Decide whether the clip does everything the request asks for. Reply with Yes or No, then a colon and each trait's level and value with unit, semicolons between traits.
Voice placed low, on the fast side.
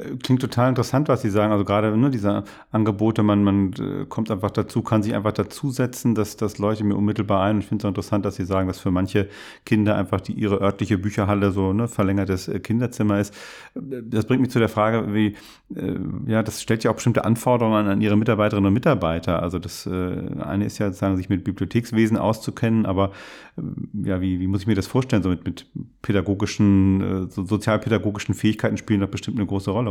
Yes: low, 105 Hz; fast, 215 wpm